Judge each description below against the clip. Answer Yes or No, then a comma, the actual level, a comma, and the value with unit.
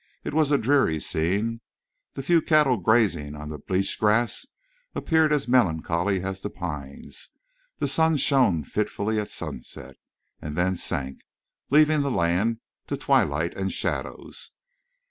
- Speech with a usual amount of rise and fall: No, wide, 8.2 semitones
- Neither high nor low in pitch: No, low, 100 Hz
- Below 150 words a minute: Yes, average, 140 wpm